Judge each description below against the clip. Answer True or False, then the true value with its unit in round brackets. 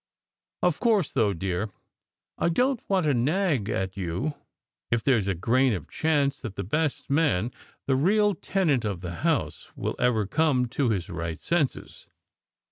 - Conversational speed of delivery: True (170 wpm)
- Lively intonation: True (8.3 semitones)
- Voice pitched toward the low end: True (130 Hz)